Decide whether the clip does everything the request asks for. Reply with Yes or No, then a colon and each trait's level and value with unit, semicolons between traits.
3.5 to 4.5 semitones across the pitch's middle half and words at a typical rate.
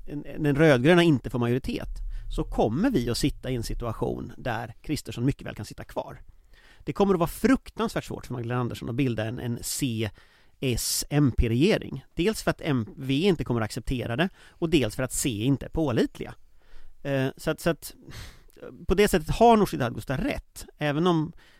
No: average, 5.3 semitones; average, 185 wpm